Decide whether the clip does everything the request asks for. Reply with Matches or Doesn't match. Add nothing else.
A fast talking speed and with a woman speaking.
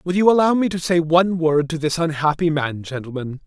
Doesn't match